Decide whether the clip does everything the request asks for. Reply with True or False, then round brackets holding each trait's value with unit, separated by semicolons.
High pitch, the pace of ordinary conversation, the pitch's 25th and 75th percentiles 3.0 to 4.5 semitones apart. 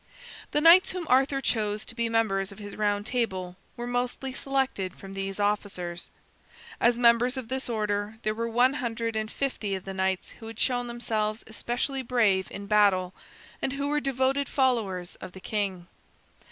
True (225 Hz; 175 wpm; 3.9 semitones)